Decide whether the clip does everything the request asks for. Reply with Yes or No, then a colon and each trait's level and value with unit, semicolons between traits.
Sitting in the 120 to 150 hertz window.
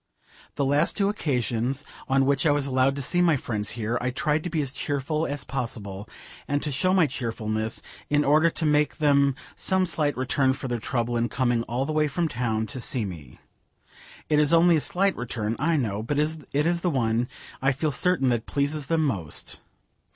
Yes: medium, 140 Hz